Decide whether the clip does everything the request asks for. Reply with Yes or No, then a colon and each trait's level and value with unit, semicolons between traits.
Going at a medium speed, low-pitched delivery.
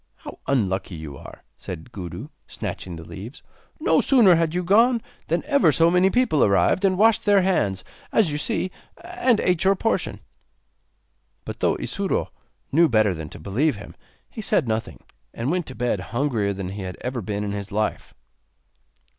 Yes: average, 175 wpm; low, 130 Hz